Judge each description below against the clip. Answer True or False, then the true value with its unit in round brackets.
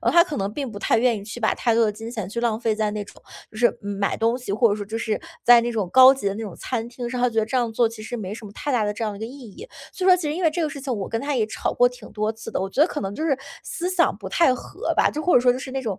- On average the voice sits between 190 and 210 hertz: False (235 Hz)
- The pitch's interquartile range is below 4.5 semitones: True (3.5 semitones)